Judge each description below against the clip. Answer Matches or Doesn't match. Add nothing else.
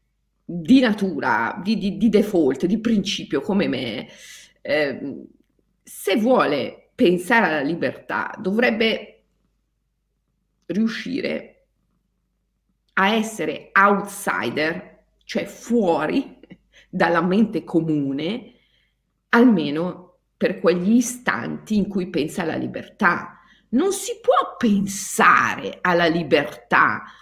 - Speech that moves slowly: Matches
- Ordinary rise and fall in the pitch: Matches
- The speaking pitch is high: Matches